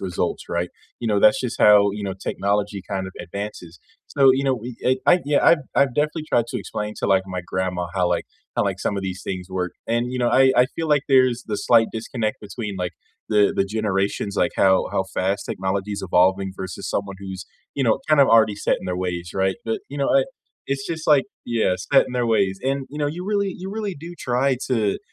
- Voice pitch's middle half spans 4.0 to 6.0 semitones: Yes, wide, 5.6 semitones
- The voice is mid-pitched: No, low, 105 Hz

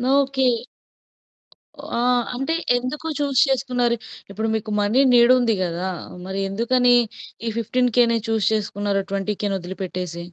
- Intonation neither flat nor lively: Yes, average, 4.0 semitones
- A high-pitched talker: Yes, high, 230 Hz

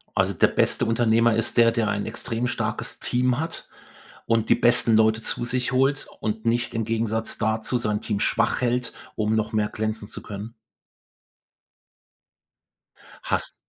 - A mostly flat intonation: Yes, narrow, 1.6 semitones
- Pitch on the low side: Yes, low, 115 Hz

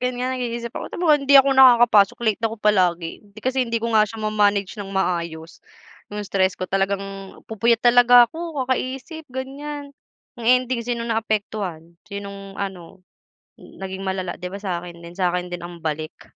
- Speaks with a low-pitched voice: No, high, 210 Hz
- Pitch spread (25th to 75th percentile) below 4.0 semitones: No, average, 4.7 semitones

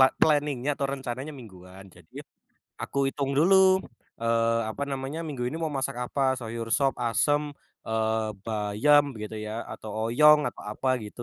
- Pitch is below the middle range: Yes, low, 130 Hz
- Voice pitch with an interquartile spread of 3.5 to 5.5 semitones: Yes, average, 4.5 semitones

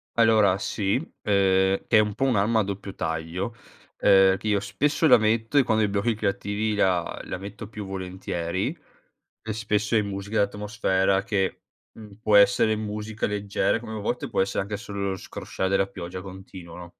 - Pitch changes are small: Yes, narrow, 2.1 semitones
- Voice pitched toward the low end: Yes, low, 100 Hz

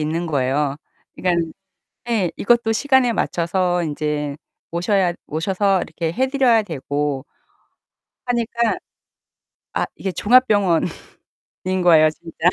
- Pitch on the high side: No, medium, 175 Hz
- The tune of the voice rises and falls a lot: Yes, wide, 6.1 semitones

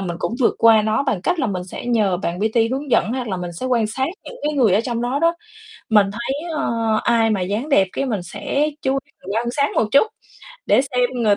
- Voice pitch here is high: Yes, high, 230 Hz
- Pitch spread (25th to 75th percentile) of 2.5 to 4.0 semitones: No, average, 4.7 semitones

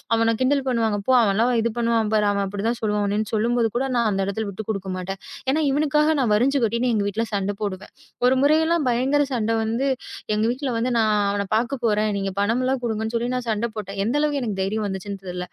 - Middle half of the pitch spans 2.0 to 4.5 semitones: Yes, average, 3.6 semitones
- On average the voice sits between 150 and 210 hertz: No, high, 225 Hz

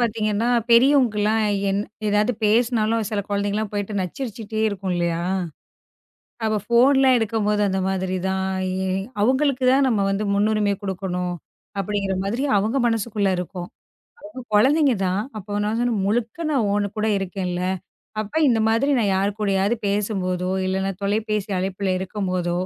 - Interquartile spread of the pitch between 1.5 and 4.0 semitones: Yes, average, 2.9 semitones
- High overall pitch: Yes, high, 210 Hz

